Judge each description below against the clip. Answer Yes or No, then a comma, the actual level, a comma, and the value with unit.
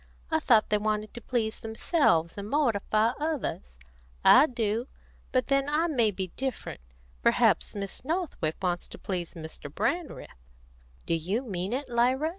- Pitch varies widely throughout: Yes, wide, 6.2 semitones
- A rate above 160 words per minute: No, average, 150 wpm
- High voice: Yes, high, 225 Hz